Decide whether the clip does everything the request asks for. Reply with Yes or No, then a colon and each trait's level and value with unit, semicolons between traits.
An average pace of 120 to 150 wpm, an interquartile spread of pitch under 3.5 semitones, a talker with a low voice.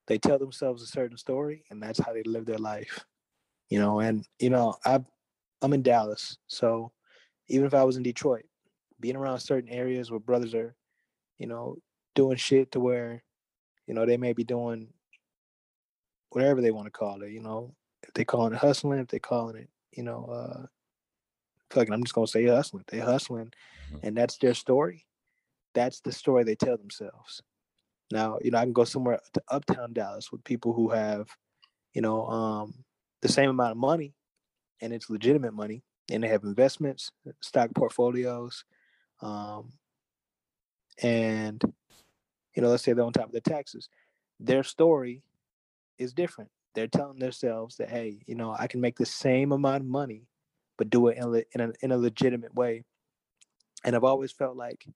No: average, 180 wpm; average, 2.7 semitones; low, 120 Hz